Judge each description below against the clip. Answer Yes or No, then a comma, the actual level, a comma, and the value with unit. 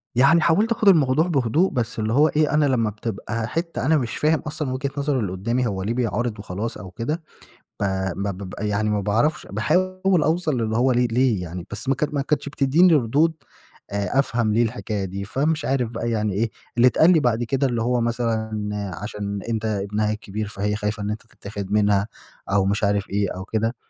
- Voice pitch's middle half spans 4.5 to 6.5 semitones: Yes, average, 5.0 semitones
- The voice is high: No, low, 115 Hz